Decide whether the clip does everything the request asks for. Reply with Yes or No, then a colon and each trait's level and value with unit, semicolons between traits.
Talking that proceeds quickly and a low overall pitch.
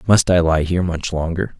Yes: fast, 225 wpm; very low, 85 Hz